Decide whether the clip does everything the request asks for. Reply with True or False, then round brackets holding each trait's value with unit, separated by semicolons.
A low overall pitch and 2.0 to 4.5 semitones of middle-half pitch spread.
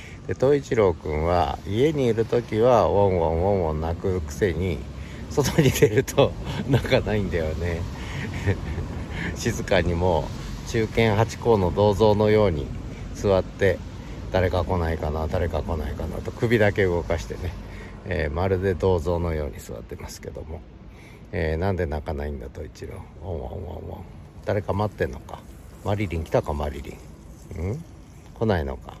True (90 Hz; 4.2 semitones)